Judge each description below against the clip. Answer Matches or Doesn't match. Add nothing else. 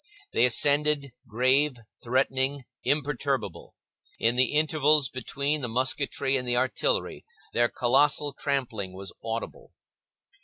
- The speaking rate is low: Matches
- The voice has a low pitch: Matches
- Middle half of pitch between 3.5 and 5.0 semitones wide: Doesn't match